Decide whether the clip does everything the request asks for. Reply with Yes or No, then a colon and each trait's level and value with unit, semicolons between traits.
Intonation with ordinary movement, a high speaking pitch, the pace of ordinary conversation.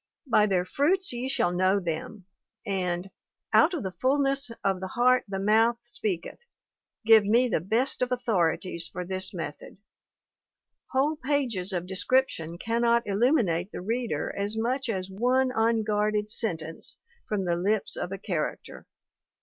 Yes: average, 5.0 semitones; high, 210 Hz; average, 150 wpm